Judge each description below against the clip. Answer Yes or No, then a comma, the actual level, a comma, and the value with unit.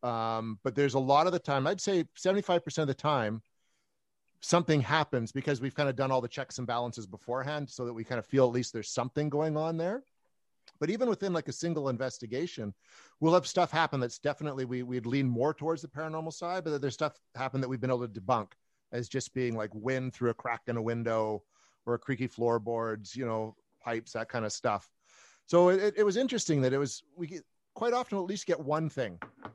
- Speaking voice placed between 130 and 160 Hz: Yes, low, 135 Hz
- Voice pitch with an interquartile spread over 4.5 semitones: Yes, average, 4.9 semitones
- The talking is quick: Yes, fast, 225 wpm